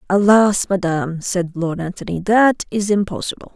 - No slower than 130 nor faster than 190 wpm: Yes, slow, 135 wpm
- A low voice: No, high, 190 Hz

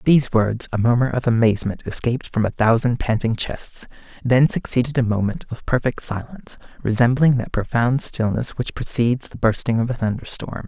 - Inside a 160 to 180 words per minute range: Yes, average, 175 wpm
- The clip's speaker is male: Yes, male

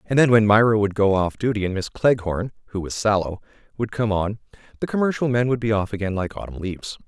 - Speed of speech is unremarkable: No, fast, 230 wpm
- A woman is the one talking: No, male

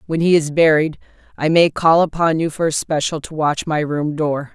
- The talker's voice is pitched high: No, medium, 155 Hz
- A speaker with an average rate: No, fast, 225 wpm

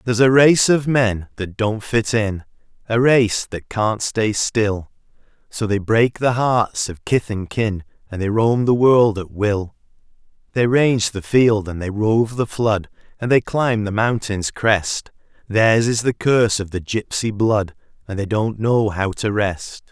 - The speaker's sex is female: No, male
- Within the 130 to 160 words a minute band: No, average, 185 wpm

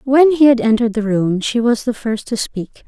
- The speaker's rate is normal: No, fast, 250 wpm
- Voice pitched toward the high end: Yes, high, 235 Hz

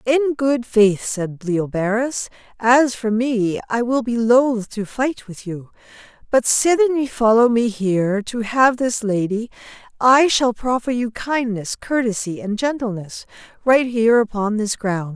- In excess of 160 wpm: No, average, 155 wpm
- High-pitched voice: Yes, high, 230 Hz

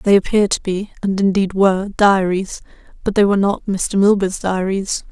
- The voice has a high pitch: Yes, high, 195 Hz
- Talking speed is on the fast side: No, average, 175 wpm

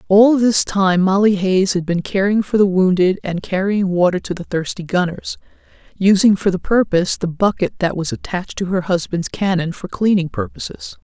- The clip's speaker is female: Yes, female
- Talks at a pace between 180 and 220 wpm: Yes, average, 185 wpm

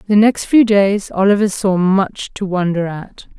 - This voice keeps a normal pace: Yes, average, 175 wpm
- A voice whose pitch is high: Yes, high, 195 Hz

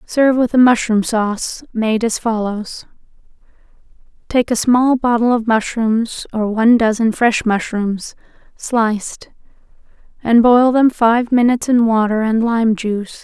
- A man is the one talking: No, female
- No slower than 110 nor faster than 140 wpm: Yes, slow, 135 wpm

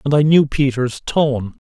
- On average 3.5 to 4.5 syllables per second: Yes, 4.1 syllables/s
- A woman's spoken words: No, male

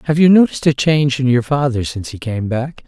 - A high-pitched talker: No, low, 135 Hz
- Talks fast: Yes, fast, 250 wpm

